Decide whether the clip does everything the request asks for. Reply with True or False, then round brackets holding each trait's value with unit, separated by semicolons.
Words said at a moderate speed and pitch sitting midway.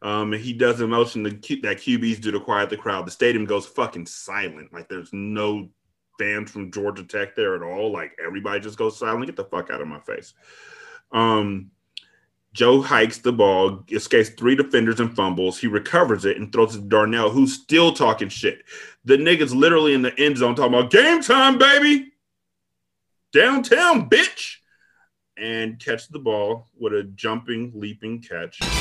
False (180 wpm; 120 Hz)